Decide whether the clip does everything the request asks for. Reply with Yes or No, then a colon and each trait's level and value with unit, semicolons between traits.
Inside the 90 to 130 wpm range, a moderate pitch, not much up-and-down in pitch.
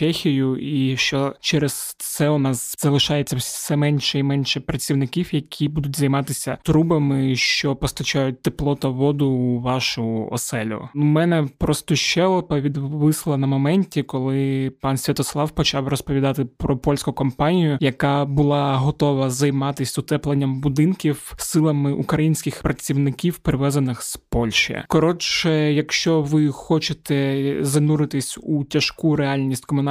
Yes: average, 120 wpm; medium, 145 Hz; narrow, 1.9 semitones